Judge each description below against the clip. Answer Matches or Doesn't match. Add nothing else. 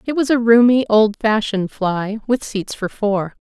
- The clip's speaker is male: Doesn't match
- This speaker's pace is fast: Doesn't match